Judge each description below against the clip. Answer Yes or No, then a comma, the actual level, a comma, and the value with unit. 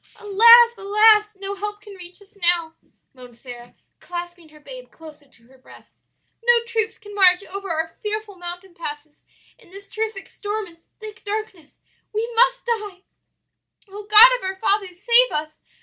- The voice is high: Yes, very high, 395 Hz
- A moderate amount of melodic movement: Yes, average, 3.9 semitones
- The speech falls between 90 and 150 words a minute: No, average, 165 wpm